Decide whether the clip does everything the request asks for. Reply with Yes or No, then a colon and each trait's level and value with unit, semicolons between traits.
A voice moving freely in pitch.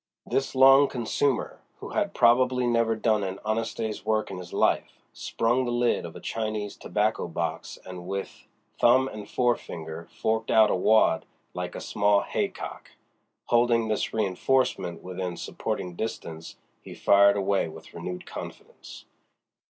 No: average, 4.2 semitones